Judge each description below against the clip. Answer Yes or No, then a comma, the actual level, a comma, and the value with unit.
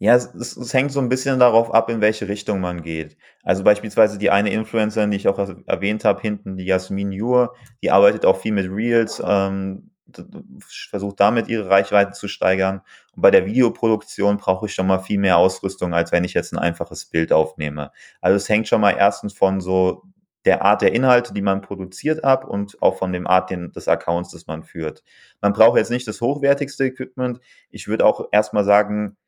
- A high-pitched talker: No, low, 100 Hz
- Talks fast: Yes, fast, 205 wpm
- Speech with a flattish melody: No, average, 3.2 semitones